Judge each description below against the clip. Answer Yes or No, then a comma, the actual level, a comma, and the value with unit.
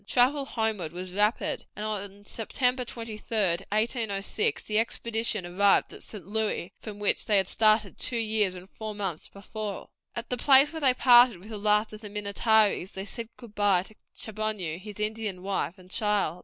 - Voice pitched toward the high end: Yes, high, 210 Hz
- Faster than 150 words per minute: Yes, average, 175 wpm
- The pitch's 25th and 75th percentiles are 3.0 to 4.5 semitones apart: No, narrow, 2.4 semitones